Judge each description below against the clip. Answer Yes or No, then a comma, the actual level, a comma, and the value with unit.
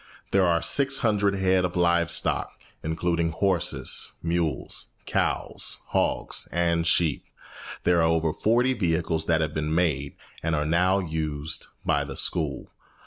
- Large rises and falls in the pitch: No, narrow, 2.4 semitones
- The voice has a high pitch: No, very low, 85 Hz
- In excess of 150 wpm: No, average, 140 wpm